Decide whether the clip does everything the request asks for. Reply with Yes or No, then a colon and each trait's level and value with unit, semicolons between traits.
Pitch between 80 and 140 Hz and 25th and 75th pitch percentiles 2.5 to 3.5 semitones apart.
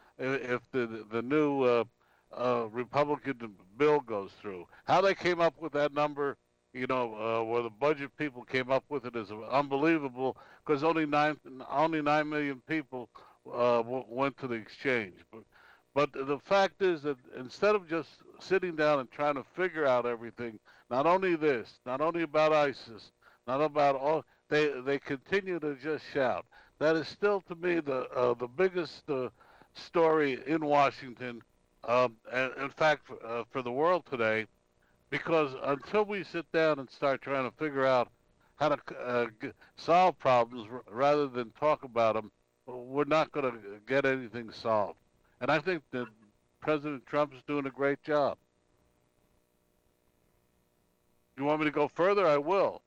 No: low, 135 Hz; average, 4.2 semitones